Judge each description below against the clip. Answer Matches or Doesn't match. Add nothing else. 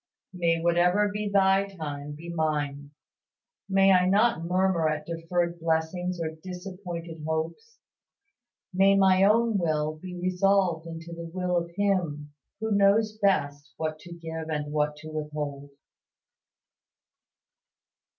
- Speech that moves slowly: Matches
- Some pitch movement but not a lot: Matches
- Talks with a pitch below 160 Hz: Doesn't match